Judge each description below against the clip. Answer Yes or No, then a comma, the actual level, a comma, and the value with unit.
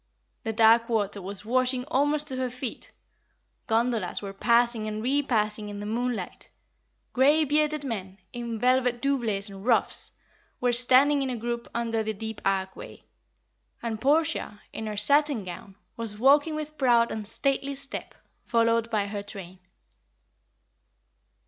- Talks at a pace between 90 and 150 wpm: Yes, average, 145 wpm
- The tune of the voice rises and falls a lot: No, average, 3.7 semitones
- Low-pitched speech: No, high, 235 Hz